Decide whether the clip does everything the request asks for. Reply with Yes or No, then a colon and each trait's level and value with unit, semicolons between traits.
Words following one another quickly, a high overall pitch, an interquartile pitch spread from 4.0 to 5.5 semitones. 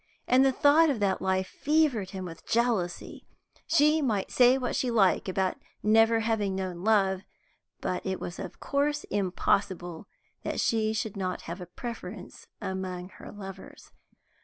No: average, 155 wpm; high, 205 Hz; average, 4.5 semitones